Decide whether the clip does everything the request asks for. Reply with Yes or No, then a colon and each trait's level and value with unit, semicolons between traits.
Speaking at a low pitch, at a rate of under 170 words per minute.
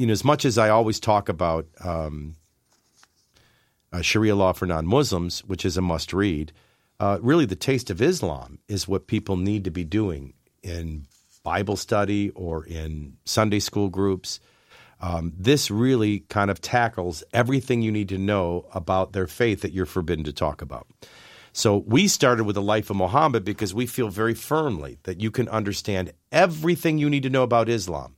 No: low, 100 Hz; average, 180 wpm